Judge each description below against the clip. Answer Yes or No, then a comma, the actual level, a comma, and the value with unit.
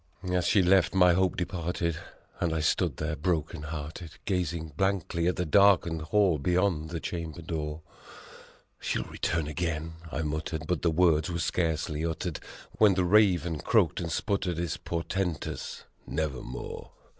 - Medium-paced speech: Yes, average, 155 wpm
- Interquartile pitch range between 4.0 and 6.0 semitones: No, narrow, 2.4 semitones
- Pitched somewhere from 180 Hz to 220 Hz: No, very low, 85 Hz